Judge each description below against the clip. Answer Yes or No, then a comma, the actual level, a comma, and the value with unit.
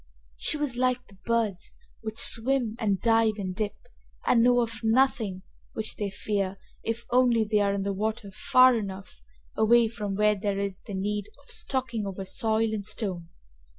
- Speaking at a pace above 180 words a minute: No, average, 175 wpm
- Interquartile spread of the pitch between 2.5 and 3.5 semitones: Yes, average, 2.8 semitones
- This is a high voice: Yes, high, 220 Hz